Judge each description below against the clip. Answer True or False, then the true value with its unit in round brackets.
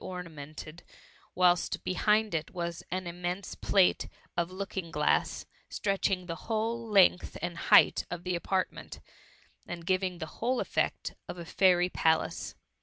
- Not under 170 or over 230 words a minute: False (145 wpm)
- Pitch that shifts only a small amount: True (2.1 semitones)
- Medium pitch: True (180 Hz)